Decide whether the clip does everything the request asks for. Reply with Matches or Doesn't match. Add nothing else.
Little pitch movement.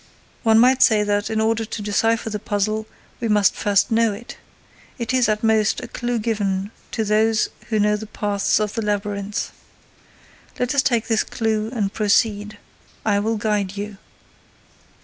Matches